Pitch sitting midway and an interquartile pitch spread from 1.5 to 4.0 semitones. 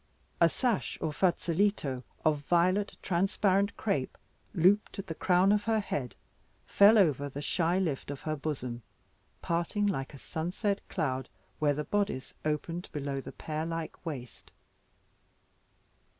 No: medium, 165 Hz; wide, 5.4 semitones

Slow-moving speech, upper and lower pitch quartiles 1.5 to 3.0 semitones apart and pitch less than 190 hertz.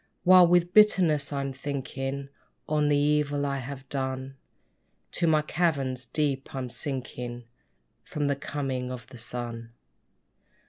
Yes: slow, 130 wpm; narrow, 2.5 semitones; medium, 140 Hz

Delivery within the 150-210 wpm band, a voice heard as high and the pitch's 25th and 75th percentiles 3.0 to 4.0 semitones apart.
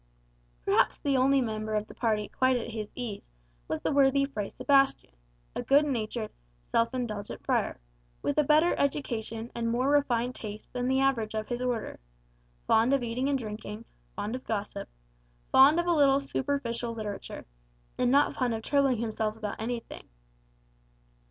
Yes: average, 165 wpm; high, 245 Hz; average, 3.7 semitones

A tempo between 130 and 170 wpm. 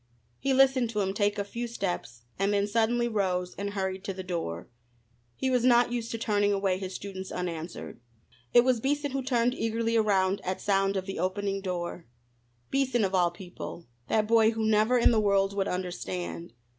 No: average, 190 wpm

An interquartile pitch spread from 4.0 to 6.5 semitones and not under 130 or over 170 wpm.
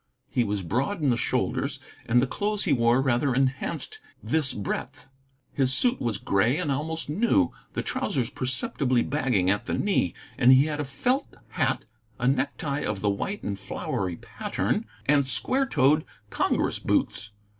Yes: average, 4.6 semitones; average, 165 wpm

